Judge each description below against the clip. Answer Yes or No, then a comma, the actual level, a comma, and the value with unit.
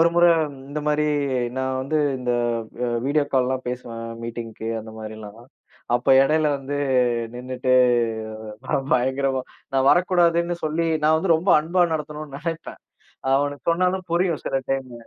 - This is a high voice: No, medium, 140 Hz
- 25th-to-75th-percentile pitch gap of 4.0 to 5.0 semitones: Yes, average, 4.3 semitones